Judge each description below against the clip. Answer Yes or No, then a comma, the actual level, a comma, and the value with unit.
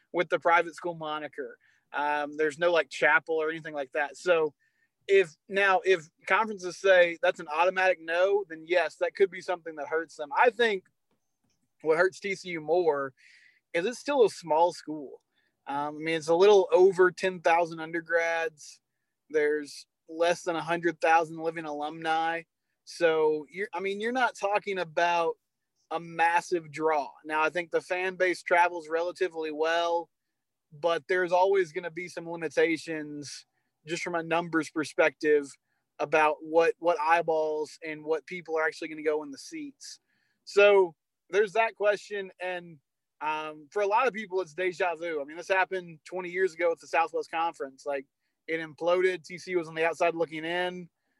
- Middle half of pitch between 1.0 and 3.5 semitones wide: Yes, average, 2.8 semitones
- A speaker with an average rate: Yes, average, 170 wpm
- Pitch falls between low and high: Yes, medium, 170 Hz